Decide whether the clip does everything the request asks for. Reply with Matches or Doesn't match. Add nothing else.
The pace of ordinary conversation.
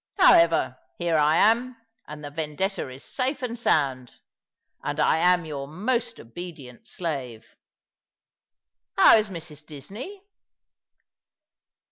Doesn't match